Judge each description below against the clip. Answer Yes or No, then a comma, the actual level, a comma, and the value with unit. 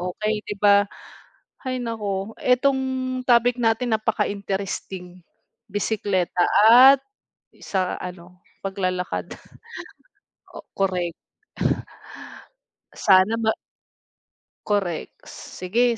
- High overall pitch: Yes, high, 200 Hz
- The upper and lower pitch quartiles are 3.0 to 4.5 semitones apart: Yes, average, 3.7 semitones